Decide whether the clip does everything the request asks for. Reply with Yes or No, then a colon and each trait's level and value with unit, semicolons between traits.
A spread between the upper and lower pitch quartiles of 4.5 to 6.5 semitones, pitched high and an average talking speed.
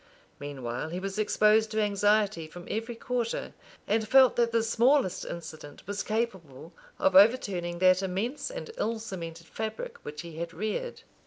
Yes: average, 4.8 semitones; high, 205 Hz; average, 155 wpm